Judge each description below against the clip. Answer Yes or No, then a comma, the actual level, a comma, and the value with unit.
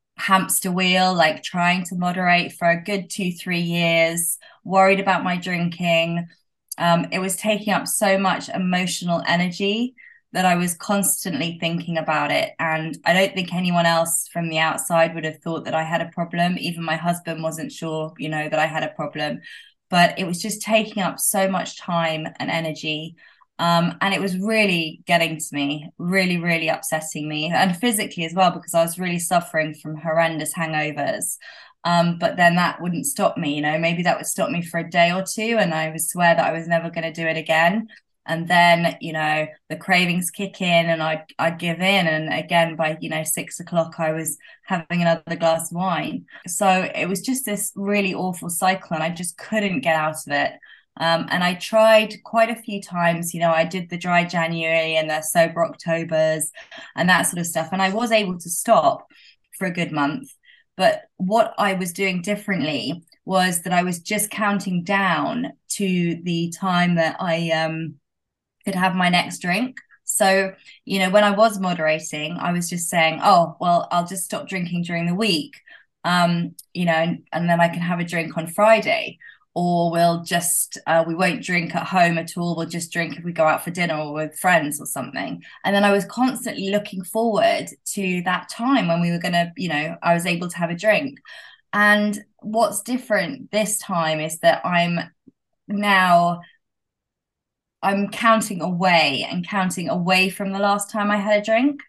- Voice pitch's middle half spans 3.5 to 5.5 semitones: No, average, 2.9 semitones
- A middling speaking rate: Yes, average, 195 wpm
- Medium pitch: Yes, medium, 175 Hz